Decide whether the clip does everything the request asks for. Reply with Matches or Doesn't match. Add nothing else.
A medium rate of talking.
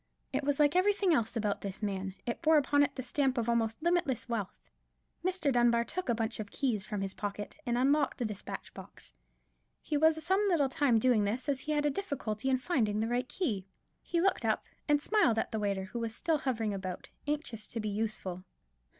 Doesn't match